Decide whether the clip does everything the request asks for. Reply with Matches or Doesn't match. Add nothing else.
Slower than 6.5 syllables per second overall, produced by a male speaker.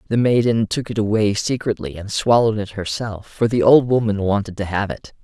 Matches